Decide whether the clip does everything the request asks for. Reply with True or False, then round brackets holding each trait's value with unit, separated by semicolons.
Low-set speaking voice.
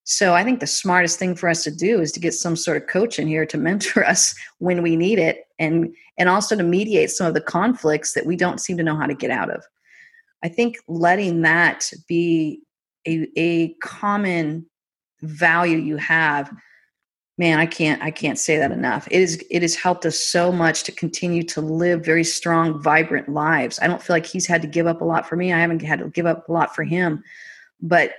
False (165 Hz)